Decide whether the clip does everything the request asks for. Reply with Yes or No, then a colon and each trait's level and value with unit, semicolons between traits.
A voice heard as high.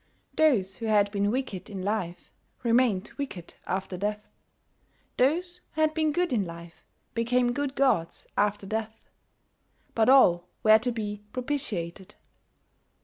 Yes: high, 220 Hz